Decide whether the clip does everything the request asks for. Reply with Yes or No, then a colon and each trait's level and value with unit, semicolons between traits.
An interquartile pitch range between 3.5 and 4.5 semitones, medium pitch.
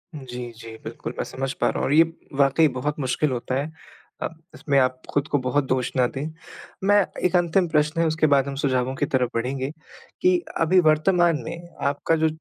Yes: average, 3.9 semitones; medium, 145 Hz